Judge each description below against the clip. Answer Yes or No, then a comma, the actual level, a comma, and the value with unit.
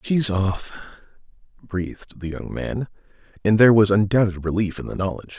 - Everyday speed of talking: Yes, average, 155 wpm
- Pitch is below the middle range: Yes, low, 100 Hz